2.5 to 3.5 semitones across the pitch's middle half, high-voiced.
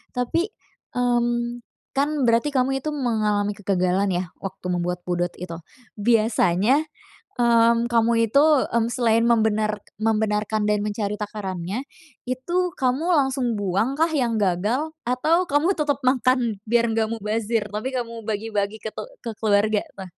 Yes: average, 3.2 semitones; high, 225 Hz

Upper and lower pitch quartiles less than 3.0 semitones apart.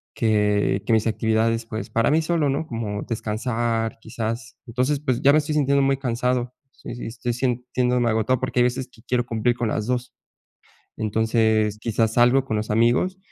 Yes: narrow, 2.4 semitones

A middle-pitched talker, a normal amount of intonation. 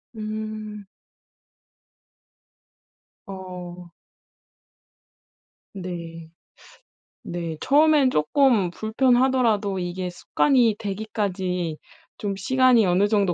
No: high, 205 Hz; average, 4.1 semitones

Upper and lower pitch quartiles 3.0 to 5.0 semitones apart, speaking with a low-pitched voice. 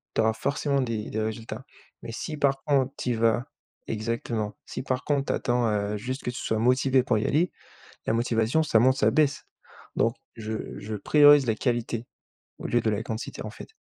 Yes: average, 3.4 semitones; low, 120 Hz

